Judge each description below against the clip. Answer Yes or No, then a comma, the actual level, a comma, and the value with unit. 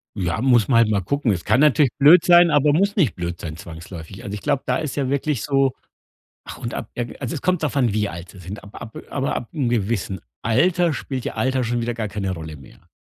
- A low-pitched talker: Yes, low, 120 Hz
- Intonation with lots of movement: Yes, wide, 6.3 semitones